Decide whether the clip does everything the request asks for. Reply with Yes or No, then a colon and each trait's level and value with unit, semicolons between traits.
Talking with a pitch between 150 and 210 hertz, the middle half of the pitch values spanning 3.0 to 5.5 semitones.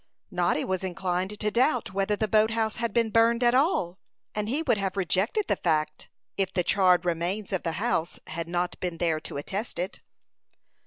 Yes: high, 190 Hz; average, 3.9 semitones